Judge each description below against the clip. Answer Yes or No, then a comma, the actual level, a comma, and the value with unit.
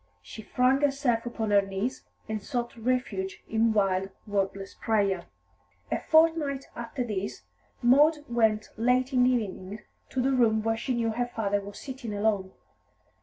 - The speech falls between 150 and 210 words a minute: Yes, average, 155 wpm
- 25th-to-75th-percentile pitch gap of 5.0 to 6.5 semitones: No, average, 3.8 semitones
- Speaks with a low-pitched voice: No, high, 225 Hz